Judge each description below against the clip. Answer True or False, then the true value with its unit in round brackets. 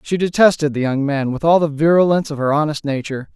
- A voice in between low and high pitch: True (150 Hz)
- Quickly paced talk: True (235 wpm)